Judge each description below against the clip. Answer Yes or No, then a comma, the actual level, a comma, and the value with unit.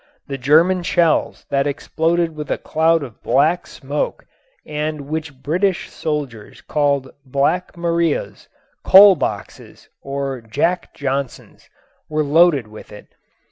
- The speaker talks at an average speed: No, slow, 120 wpm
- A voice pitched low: No, medium, 150 Hz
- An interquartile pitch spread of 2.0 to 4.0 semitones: Yes, average, 3.4 semitones